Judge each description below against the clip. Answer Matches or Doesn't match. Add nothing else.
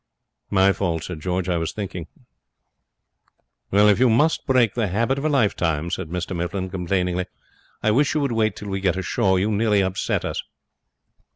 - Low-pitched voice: Matches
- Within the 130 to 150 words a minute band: Doesn't match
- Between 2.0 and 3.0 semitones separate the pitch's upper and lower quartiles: Doesn't match